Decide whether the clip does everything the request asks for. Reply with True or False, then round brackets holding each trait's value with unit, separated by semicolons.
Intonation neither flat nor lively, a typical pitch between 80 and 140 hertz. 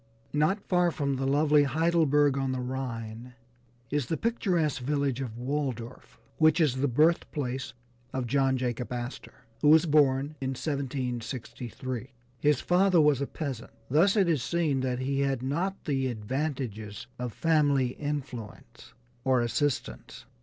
True (3.2 semitones; 135 Hz)